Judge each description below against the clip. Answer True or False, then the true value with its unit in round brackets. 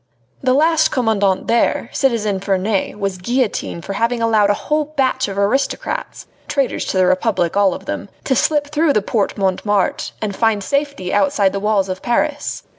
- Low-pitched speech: False (215 Hz)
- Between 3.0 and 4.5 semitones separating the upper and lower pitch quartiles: False (5.5 semitones)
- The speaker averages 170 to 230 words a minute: True (180 wpm)